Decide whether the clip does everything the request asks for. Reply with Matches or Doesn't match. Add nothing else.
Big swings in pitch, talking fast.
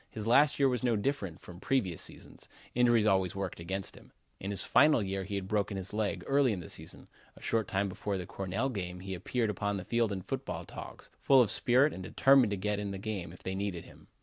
Doesn't match